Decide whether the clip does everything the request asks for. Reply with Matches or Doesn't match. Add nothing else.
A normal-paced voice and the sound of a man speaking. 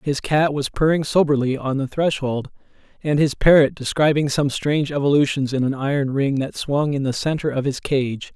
Matches